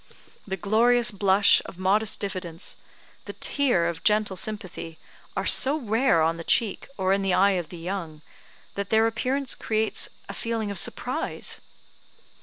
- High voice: Yes, high, 200 Hz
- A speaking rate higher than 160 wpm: No, average, 155 wpm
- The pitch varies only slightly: No, average, 3.3 semitones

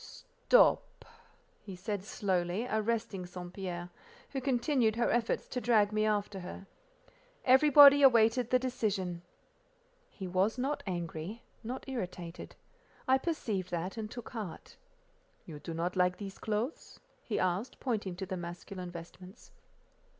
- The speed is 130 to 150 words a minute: Yes, slow, 135 wpm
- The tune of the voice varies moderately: Yes, average, 5.0 semitones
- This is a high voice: Yes, high, 205 Hz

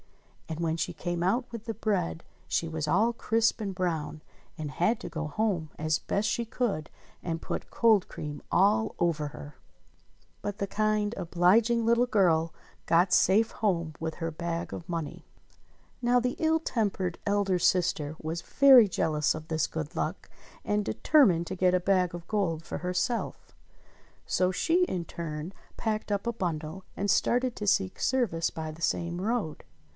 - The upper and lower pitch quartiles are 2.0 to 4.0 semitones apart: No, average, 4.8 semitones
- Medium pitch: Yes, medium, 180 Hz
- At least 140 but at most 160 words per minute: No, average, 170 wpm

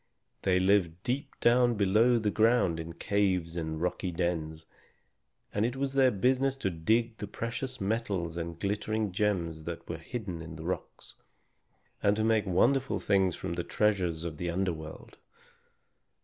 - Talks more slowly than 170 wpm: Yes, average, 160 wpm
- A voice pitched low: Yes, very low, 95 Hz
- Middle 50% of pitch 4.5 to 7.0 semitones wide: Yes, average, 5.0 semitones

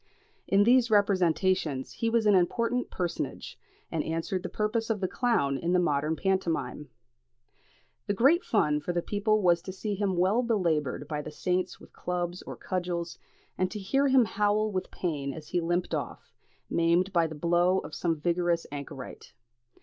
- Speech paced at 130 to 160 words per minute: No, average, 170 wpm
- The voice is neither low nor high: Yes, medium, 180 Hz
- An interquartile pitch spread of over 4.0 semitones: No, average, 3.7 semitones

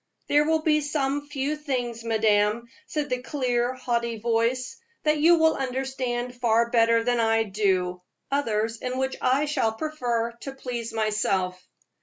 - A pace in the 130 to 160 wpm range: Yes, average, 150 wpm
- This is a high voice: Yes, high, 245 Hz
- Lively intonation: No, average, 3.2 semitones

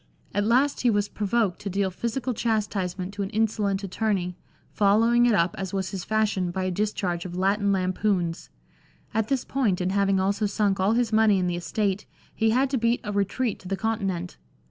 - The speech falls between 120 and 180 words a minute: No, average, 195 wpm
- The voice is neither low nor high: No, high, 200 Hz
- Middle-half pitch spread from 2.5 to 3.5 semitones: Yes, average, 2.8 semitones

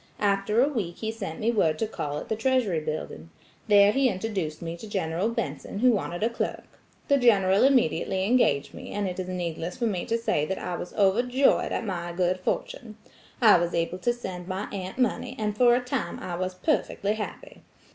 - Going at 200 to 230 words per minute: Yes, fast, 205 wpm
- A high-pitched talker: Yes, high, 200 Hz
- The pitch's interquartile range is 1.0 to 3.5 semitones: No, average, 4.5 semitones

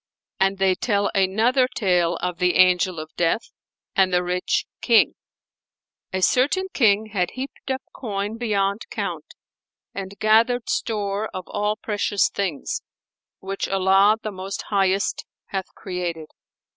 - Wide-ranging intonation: No, average, 2.7 semitones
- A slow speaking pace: Yes, slow, 130 wpm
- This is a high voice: Yes, high, 195 Hz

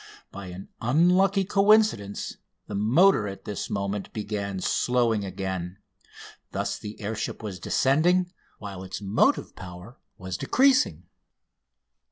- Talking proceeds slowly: Yes, slow, 120 wpm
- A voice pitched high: No, low, 105 Hz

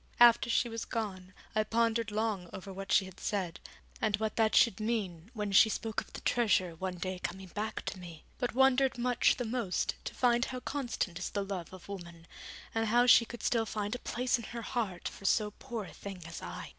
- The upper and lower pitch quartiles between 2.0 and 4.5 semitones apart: Yes, average, 3.9 semitones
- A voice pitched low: No, high, 215 Hz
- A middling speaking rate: No, fast, 220 wpm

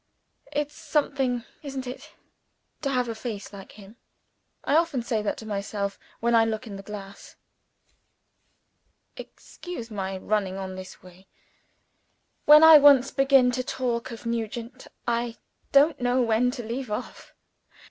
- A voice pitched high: Yes, high, 235 Hz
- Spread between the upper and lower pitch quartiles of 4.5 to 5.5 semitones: No, average, 4.0 semitones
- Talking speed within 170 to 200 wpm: No, average, 145 wpm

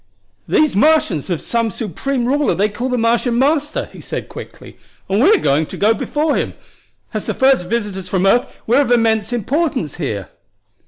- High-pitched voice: Yes, high, 235 Hz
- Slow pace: No, average, 170 wpm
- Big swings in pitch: Yes, wide, 5.9 semitones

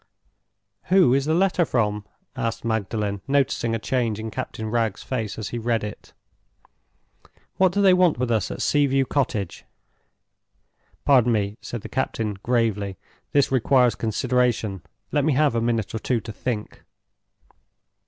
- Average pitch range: Yes, average, 3.7 semitones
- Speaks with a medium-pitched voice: No, low, 120 Hz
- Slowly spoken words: No, average, 155 wpm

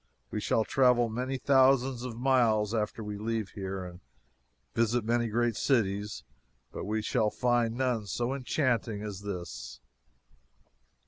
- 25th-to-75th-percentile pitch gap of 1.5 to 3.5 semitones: Yes, average, 2.9 semitones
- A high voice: No, low, 115 Hz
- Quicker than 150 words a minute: No, slow, 135 wpm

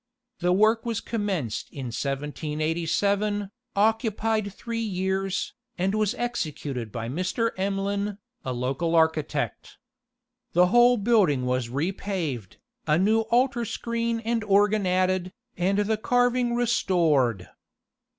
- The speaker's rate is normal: No, slow, 110 wpm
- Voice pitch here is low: No, high, 195 Hz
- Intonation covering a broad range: Yes, wide, 6.1 semitones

